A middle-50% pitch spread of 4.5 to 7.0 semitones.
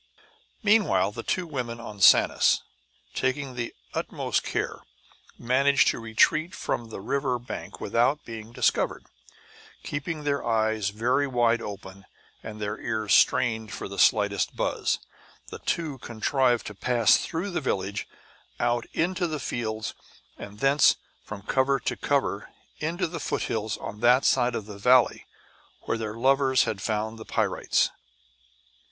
No: average, 4.0 semitones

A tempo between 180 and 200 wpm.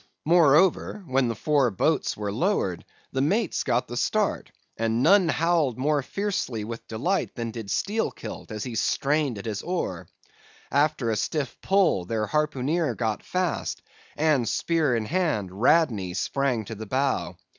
No: average, 155 wpm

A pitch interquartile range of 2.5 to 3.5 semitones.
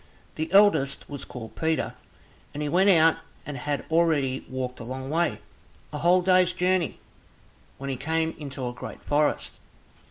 No: average, 4.2 semitones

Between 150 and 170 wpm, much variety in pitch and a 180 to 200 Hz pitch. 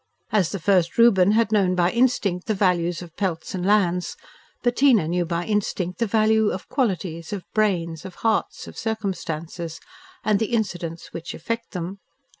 No: average, 165 wpm; average, 3.9 semitones; high, 190 Hz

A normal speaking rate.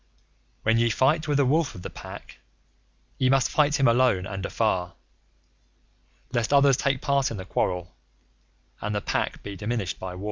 Yes: average, 175 wpm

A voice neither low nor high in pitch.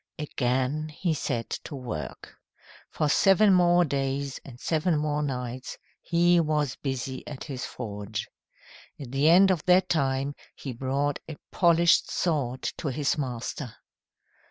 Yes: medium, 145 Hz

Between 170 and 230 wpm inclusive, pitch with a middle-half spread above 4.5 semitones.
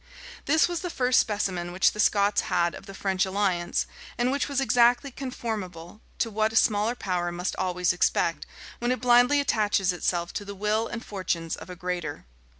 Yes: average, 185 wpm; average, 4.9 semitones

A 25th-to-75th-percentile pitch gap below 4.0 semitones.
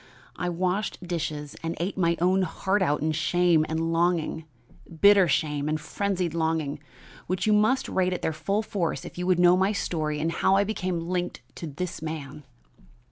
Yes: average, 2.8 semitones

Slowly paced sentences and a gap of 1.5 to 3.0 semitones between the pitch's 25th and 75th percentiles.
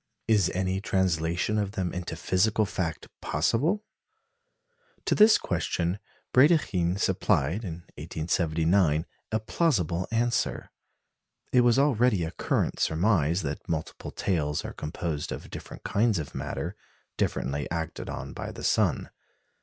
No: slow, 125 wpm; average, 5.1 semitones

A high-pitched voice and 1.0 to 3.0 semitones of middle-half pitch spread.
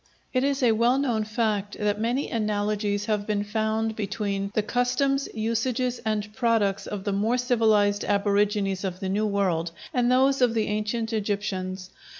Yes: high, 215 Hz; narrow, 2.5 semitones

